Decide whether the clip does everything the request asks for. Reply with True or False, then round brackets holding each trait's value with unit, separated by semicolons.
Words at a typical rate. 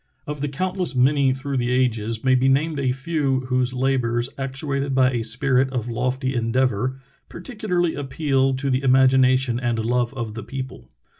True (170 wpm)